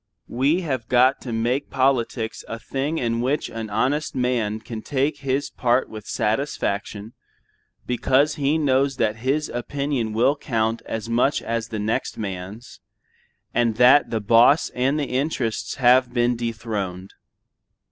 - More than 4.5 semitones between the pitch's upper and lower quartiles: No, average, 3.4 semitones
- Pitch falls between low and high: No, low, 120 Hz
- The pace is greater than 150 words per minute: No, average, 145 wpm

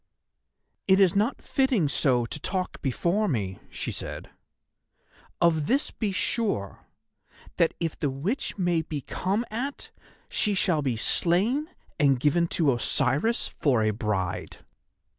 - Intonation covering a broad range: Yes, wide, 7.4 semitones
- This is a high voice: No, medium, 170 Hz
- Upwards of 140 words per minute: No, slow, 135 wpm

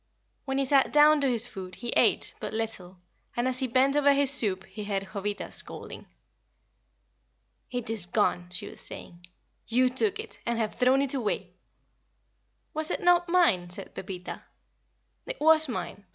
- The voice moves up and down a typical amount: No, wide, 6.0 semitones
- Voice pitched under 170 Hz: No, high, 245 Hz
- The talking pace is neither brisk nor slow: Yes, average, 165 wpm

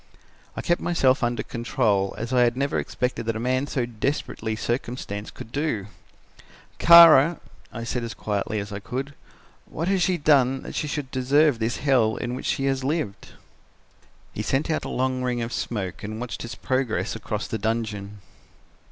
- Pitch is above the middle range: No, low, 125 Hz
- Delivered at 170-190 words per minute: Yes, average, 180 wpm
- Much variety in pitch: No, average, 3.7 semitones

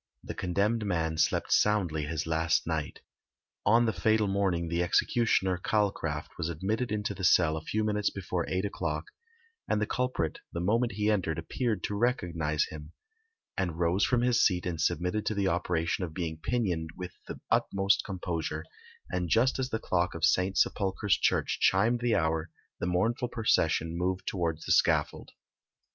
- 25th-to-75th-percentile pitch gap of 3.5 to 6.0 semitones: Yes, average, 4.3 semitones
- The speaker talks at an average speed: Yes, average, 170 wpm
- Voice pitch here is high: No, very low, 90 Hz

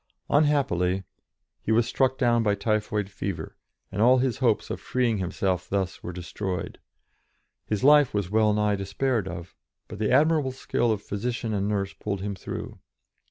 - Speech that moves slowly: No, average, 160 wpm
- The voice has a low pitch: Yes, low, 105 Hz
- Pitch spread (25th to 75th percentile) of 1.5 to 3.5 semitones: No, average, 4.2 semitones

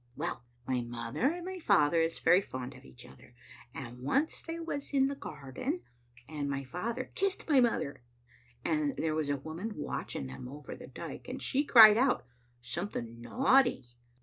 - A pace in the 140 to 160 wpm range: No, average, 175 wpm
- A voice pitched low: No, medium, 165 Hz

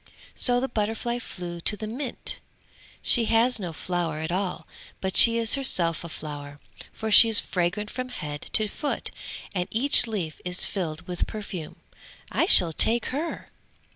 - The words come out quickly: No, average, 165 wpm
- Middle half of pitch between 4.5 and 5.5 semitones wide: Yes, average, 5.2 semitones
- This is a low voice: No, high, 205 Hz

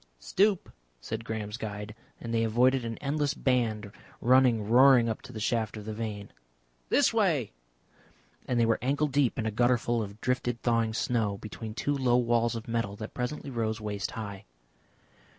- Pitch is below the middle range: Yes, low, 115 Hz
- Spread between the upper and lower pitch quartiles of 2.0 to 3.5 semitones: Yes, narrow, 2.4 semitones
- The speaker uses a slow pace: No, average, 175 wpm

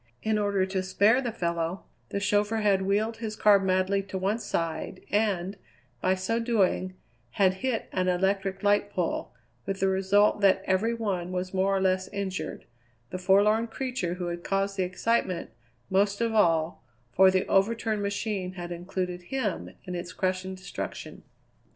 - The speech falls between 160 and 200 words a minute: Yes, average, 165 wpm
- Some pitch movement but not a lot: No, narrow, 1.9 semitones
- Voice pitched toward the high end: Yes, high, 195 Hz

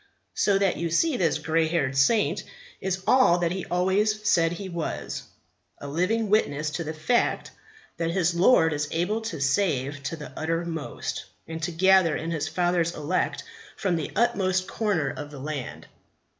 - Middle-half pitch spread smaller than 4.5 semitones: Yes, average, 3.4 semitones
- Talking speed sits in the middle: Yes, average, 170 wpm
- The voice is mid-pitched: Yes, medium, 170 Hz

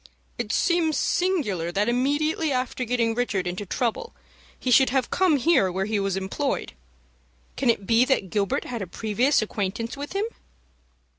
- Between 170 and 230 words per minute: No, average, 160 wpm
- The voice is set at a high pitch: Yes, high, 240 Hz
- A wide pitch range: Yes, wide, 6.1 semitones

